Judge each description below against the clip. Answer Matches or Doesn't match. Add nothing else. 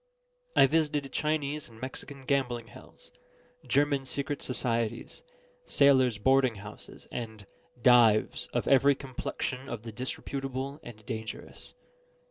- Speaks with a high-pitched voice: Doesn't match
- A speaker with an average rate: Doesn't match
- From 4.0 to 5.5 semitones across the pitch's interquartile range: Doesn't match